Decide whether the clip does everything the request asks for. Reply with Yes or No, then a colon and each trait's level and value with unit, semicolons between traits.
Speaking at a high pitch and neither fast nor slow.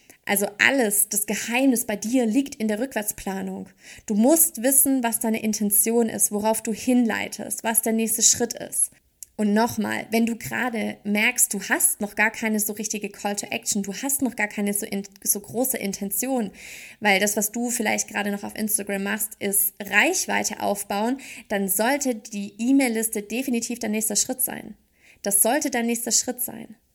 Yes: high, 220 Hz; average, 175 wpm